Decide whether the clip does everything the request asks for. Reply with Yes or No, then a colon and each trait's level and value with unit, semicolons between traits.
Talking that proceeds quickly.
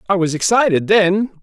No: average, 170 wpm